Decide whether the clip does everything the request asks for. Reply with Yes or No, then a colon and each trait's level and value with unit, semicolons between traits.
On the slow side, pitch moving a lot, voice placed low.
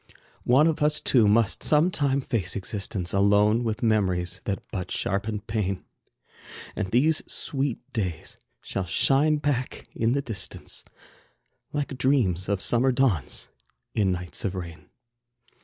Yes: slow, 130 wpm; wide, 5.8 semitones; low, 110 Hz